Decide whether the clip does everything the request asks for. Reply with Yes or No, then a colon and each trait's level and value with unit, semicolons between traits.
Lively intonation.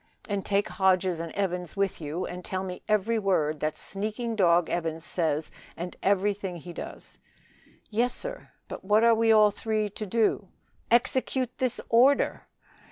No: average, 3.9 semitones